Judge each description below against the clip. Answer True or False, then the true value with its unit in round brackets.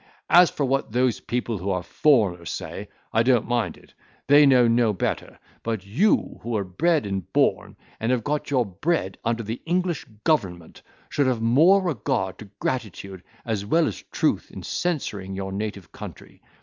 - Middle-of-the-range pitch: False (115 Hz)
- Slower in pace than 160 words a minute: False (175 wpm)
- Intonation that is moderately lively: False (6.3 semitones)